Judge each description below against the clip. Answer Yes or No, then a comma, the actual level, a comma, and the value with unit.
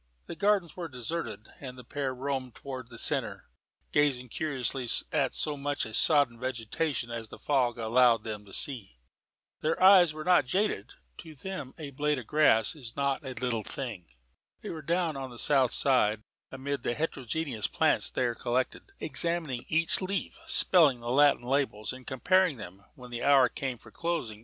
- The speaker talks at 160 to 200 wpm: Yes, average, 175 wpm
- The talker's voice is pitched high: No, low, 135 Hz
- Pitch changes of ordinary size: Yes, average, 4.3 semitones